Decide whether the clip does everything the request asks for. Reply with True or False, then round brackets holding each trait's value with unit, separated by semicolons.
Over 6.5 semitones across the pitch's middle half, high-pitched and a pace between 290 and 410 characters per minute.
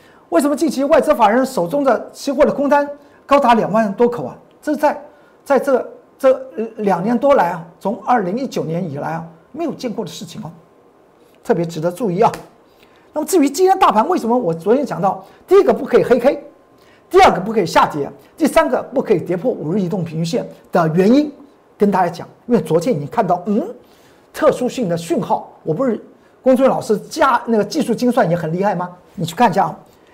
True (7.1 semitones; 240 Hz; 305 characters per minute)